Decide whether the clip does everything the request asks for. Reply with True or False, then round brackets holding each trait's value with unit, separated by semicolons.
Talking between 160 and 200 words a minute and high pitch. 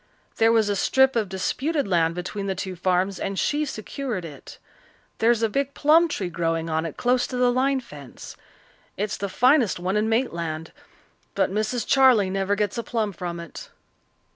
True (180 wpm; 205 Hz)